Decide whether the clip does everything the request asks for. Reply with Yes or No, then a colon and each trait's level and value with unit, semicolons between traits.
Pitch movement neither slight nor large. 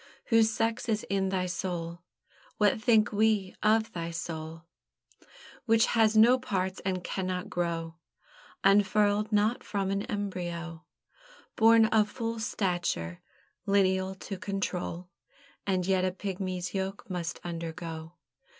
Yes: average, 3.3 semitones